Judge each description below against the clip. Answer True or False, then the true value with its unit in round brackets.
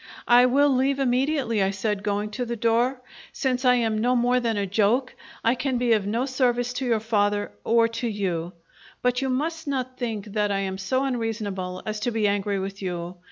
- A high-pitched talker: True (230 Hz)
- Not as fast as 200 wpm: False (205 wpm)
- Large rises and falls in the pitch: False (3.6 semitones)